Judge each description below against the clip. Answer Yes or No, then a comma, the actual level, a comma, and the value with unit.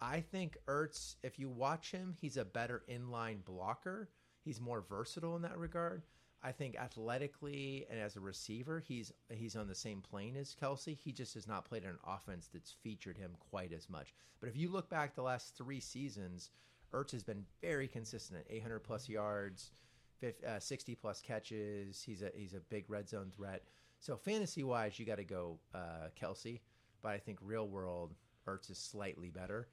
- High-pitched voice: No, low, 115 Hz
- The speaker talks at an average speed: Yes, average, 190 wpm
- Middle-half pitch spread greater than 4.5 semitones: Yes, average, 5.2 semitones